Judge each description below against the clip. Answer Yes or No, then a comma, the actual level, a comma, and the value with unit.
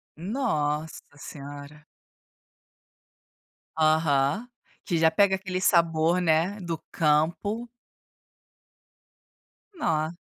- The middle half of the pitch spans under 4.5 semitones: Yes, average, 3.6 semitones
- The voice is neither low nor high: Yes, medium, 165 Hz